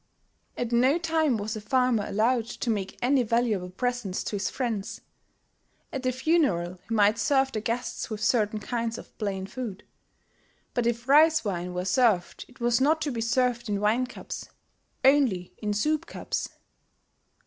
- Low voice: No, high, 235 Hz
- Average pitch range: Yes, average, 3.6 semitones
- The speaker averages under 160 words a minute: No, average, 165 wpm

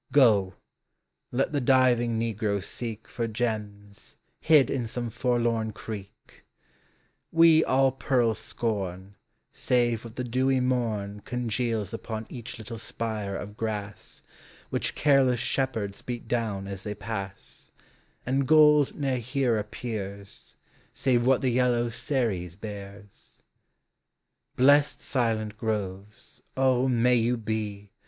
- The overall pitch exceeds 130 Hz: No, low, 115 Hz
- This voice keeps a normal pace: No, slow, 120 wpm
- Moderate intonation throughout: Yes, average, 3.4 semitones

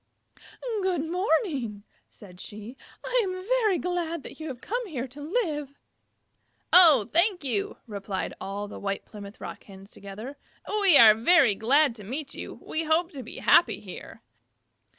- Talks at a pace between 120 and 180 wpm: Yes, average, 150 wpm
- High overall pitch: Yes, very high, 285 Hz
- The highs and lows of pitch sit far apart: Yes, wide, 8.7 semitones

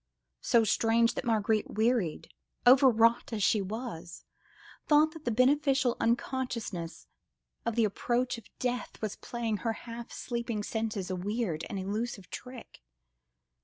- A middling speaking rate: No, slow, 130 wpm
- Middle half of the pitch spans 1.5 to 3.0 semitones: Yes, average, 2.7 semitones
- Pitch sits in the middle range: No, high, 230 Hz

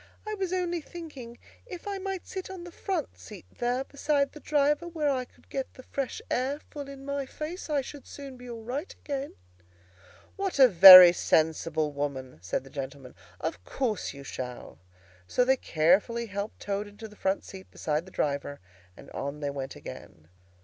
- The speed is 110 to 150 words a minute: No, average, 185 wpm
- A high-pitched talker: Yes, high, 245 Hz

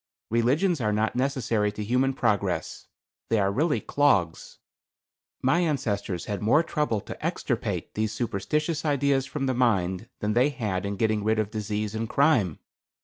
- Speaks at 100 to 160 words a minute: Yes, average, 155 wpm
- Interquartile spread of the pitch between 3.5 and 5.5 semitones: Yes, average, 5.0 semitones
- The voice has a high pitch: No, low, 115 Hz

